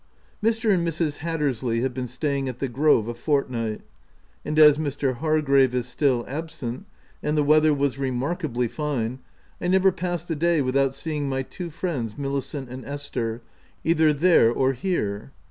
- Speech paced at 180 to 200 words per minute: No, average, 160 wpm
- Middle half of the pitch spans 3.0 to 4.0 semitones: Yes, average, 3.7 semitones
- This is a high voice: No, medium, 140 Hz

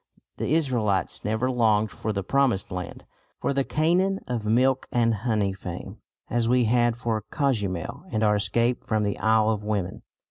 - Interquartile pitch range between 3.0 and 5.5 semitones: Yes, average, 3.3 semitones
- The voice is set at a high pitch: No, low, 110 Hz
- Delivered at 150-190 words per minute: Yes, average, 170 wpm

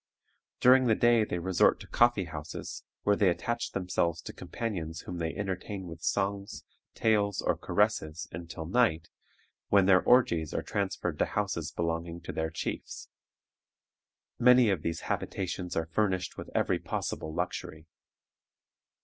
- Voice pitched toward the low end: Yes, very low, 90 Hz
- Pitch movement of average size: Yes, average, 4.0 semitones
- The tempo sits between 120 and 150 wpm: Yes, average, 140 wpm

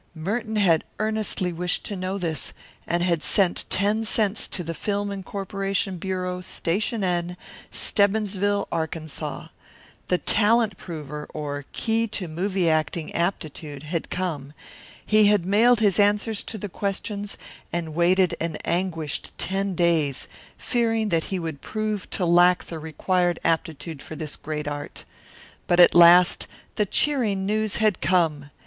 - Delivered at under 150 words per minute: Yes, average, 140 wpm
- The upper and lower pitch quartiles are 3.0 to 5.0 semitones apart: Yes, average, 3.7 semitones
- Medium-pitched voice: Yes, medium, 180 Hz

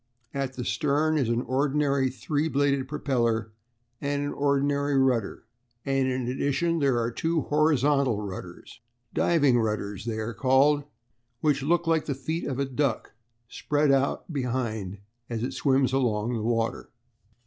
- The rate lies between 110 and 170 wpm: Yes, average, 150 wpm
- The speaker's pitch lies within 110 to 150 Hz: Yes, low, 135 Hz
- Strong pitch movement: No, average, 3.3 semitones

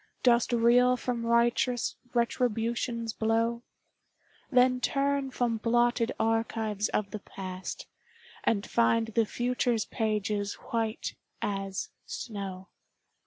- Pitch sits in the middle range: No, high, 230 Hz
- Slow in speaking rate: Yes, slow, 100 wpm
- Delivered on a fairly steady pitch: Yes, narrow, 2.1 semitones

